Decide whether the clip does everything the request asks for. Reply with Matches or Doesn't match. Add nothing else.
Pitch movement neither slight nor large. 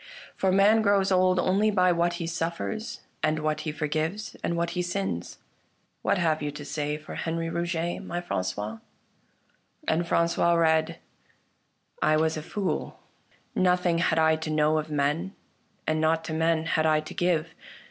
Doesn't match